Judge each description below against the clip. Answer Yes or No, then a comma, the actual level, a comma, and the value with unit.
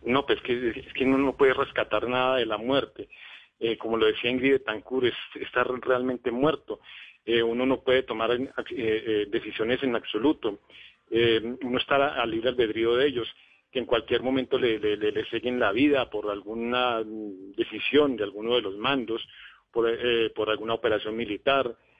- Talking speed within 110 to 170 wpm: No, average, 180 wpm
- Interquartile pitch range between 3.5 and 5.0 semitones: No, average, 2.8 semitones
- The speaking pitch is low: Yes, low, 120 Hz